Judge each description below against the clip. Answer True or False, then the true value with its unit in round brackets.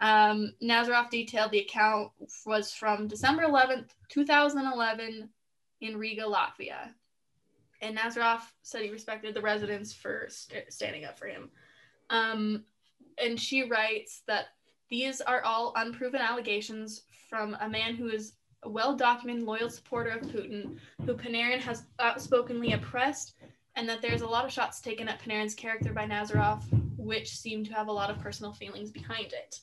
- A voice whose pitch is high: True (225 Hz)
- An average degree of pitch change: False (2.1 semitones)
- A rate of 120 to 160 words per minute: True (155 wpm)